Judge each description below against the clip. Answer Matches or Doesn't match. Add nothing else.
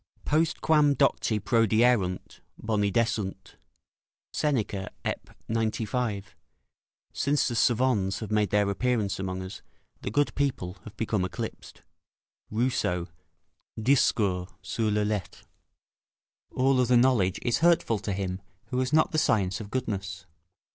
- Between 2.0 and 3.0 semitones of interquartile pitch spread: Doesn't match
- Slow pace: Matches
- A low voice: Matches